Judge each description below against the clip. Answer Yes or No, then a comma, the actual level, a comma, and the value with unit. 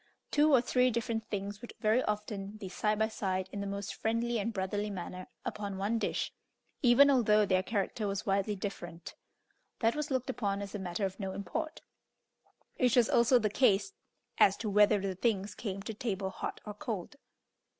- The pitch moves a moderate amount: Yes, average, 3.0 semitones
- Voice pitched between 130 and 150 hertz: No, high, 210 Hz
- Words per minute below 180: No, average, 185 wpm